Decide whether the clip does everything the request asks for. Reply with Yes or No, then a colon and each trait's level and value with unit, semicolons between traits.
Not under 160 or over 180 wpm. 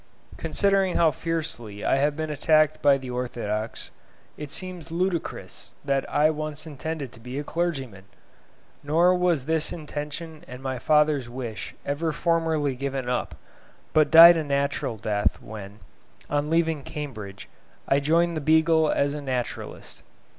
No: average, 140 wpm